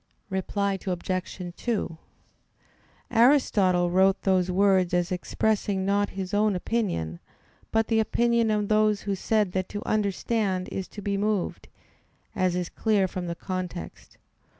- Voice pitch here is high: Yes, high, 195 Hz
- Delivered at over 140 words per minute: No, slow, 135 wpm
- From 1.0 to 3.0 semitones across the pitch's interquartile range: Yes, narrow, 2.6 semitones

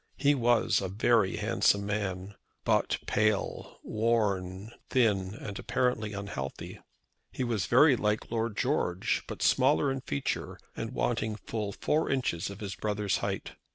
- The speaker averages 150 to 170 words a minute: No, average, 140 wpm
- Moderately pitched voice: No, low, 105 Hz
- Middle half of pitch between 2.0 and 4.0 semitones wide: Yes, average, 3.2 semitones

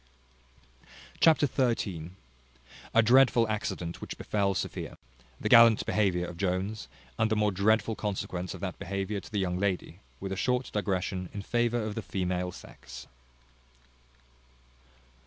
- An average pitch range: Yes, average, 3.2 semitones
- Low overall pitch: Yes, low, 100 Hz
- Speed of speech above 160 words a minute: No, average, 140 wpm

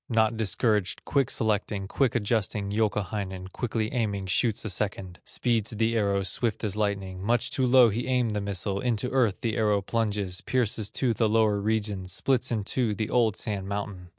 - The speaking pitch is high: No, low, 105 Hz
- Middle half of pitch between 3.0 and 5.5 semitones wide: No, narrow, 2.5 semitones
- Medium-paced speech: Yes, average, 180 wpm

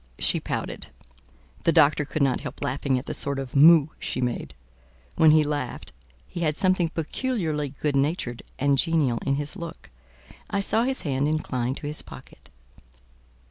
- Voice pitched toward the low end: No, medium, 150 Hz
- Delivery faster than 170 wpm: No, average, 165 wpm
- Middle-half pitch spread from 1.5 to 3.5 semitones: Yes, average, 3.1 semitones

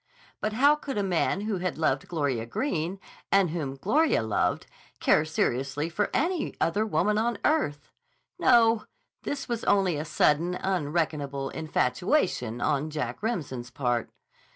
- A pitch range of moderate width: No, wide, 7.1 semitones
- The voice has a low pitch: No, medium, 170 Hz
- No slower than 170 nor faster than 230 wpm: No, average, 140 wpm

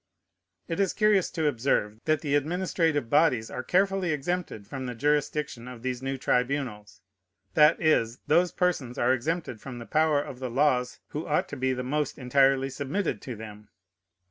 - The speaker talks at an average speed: Yes, average, 170 wpm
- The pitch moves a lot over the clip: No, average, 4.1 semitones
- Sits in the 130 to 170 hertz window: Yes, medium, 140 Hz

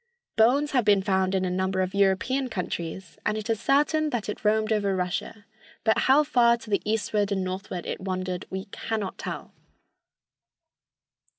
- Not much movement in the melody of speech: No, average, 3.3 semitones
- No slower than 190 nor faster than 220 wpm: No, average, 170 wpm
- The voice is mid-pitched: No, high, 205 Hz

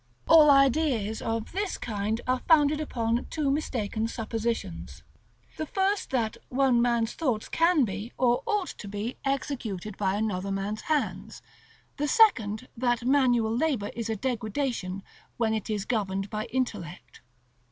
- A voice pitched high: Yes, high, 235 Hz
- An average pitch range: Yes, average, 4.4 semitones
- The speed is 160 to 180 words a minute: No, average, 140 wpm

